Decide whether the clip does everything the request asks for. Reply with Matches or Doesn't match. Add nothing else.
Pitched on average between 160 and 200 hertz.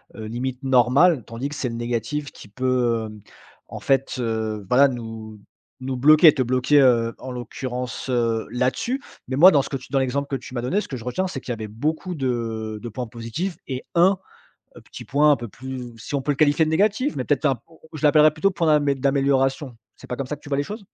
Doesn't match